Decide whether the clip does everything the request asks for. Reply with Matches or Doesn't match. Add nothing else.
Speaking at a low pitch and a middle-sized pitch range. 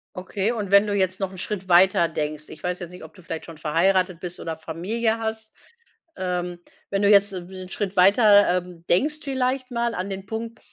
Doesn't match